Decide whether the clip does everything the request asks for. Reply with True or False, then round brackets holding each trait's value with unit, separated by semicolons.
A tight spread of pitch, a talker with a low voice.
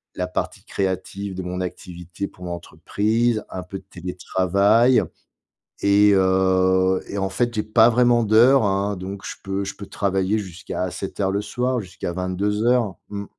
True (2.3 semitones; 100 Hz)